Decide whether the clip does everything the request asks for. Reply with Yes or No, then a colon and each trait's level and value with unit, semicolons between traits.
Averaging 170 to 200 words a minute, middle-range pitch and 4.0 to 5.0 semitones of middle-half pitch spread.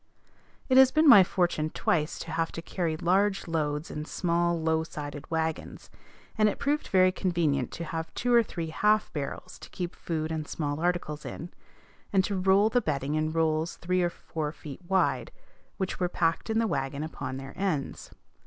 No: average, 185 wpm; medium, 165 Hz; average, 3.4 semitones